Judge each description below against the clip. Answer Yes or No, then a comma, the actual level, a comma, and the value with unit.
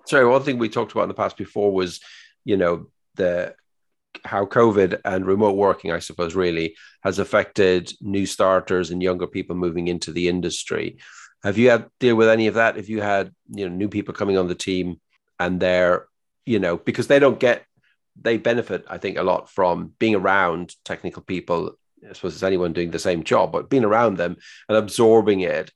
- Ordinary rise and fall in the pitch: Yes, average, 3.9 semitones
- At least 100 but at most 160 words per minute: No, average, 200 wpm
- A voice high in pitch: No, very low, 95 Hz